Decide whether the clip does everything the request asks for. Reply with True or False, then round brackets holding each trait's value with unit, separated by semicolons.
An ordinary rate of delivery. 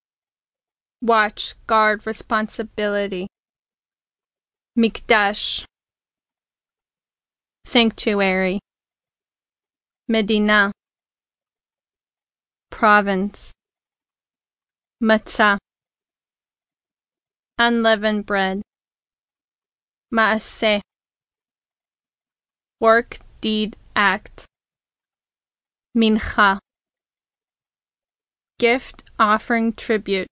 False (35 wpm)